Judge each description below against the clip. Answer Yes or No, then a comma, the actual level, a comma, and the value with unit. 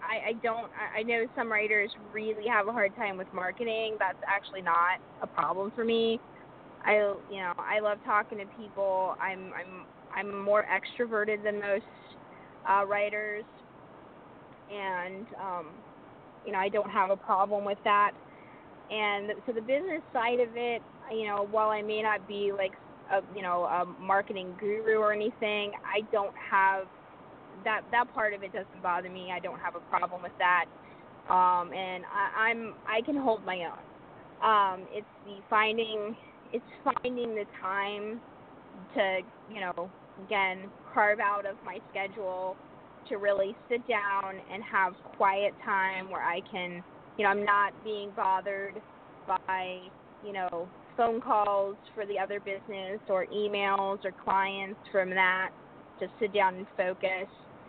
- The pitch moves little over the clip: Yes, narrow, 2.2 semitones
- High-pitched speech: Yes, high, 200 Hz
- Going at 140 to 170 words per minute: Yes, average, 160 wpm